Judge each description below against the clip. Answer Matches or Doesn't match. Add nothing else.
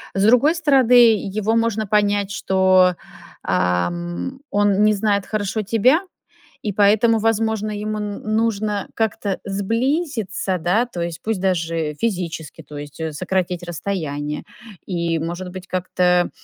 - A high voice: Matches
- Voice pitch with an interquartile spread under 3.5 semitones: Doesn't match